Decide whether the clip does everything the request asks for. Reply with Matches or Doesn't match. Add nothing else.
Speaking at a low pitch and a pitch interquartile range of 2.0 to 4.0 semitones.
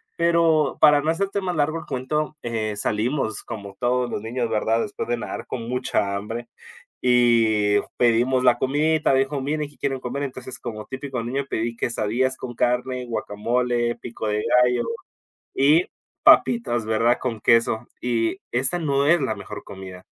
Matches